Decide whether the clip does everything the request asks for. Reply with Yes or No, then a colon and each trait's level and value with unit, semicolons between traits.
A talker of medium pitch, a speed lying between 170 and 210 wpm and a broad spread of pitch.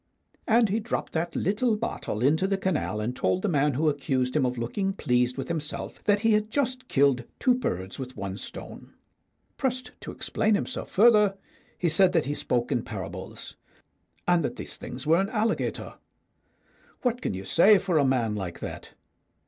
Yes: medium, 165 Hz; average, 180 wpm; wide, 8.8 semitones